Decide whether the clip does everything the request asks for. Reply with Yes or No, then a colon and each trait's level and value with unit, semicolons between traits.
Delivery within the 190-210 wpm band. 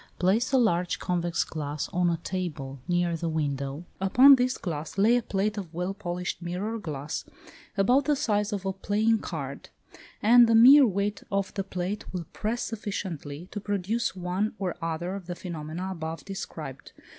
No: average, 170 wpm